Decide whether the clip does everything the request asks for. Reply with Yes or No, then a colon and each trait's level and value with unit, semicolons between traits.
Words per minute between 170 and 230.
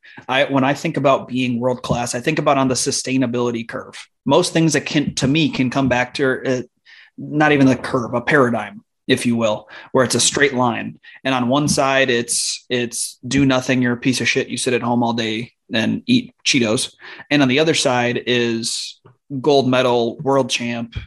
Yes: average, 200 wpm